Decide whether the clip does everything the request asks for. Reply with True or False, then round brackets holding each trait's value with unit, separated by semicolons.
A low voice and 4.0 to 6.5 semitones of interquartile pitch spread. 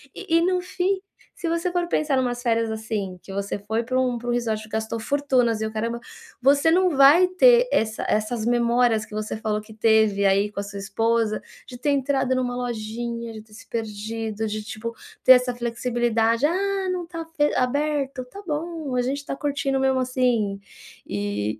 False (240 Hz; 4.5 semitones)